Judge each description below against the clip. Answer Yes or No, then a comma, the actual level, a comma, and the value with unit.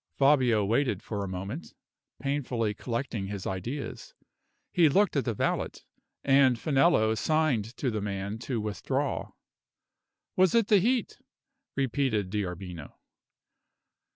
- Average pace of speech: No, slow, 120 wpm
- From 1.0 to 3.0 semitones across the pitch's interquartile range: No, wide, 5.6 semitones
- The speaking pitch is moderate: No, low, 120 Hz